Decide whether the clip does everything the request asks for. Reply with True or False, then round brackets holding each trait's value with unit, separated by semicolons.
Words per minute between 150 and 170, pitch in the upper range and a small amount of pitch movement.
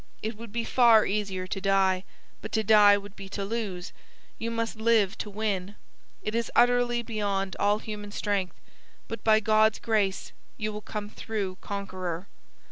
True (165 wpm; 210 Hz; 2.1 semitones)